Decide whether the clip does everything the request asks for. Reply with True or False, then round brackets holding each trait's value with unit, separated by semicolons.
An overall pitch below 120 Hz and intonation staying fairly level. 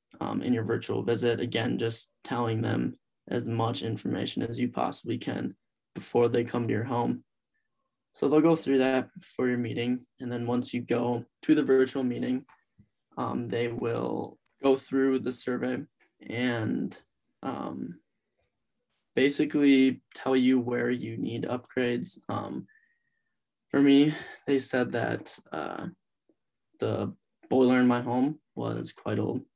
False (125 Hz; 2.0 semitones)